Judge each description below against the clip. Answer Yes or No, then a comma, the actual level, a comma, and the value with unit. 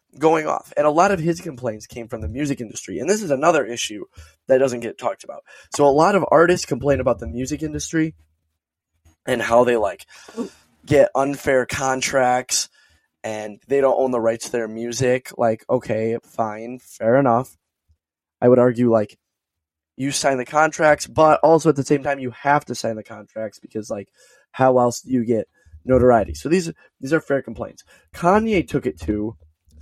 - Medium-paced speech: Yes, average, 185 wpm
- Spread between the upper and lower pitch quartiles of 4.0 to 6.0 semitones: Yes, average, 4.5 semitones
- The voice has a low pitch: Yes, low, 125 Hz